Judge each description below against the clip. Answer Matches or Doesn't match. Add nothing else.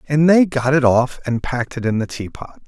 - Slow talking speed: Doesn't match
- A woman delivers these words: Doesn't match